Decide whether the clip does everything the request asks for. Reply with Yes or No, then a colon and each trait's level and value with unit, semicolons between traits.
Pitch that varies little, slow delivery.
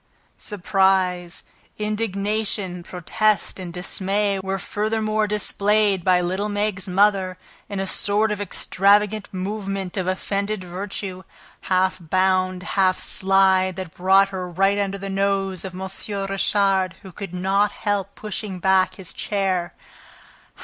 Yes: narrow, 1.7 semitones; slow, 125 wpm